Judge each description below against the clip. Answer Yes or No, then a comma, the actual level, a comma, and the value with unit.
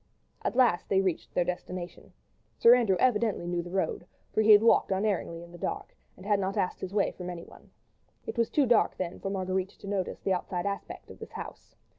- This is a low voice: No, high, 190 Hz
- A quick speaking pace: Yes, fast, 215 wpm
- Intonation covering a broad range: No, average, 2.8 semitones